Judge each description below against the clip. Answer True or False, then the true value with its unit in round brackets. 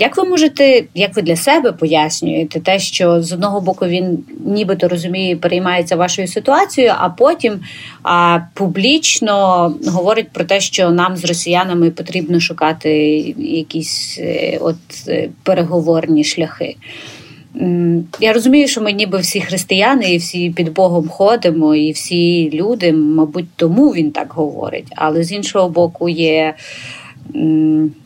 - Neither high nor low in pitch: True (175 Hz)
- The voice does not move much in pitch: False (3.3 semitones)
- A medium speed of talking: True (135 wpm)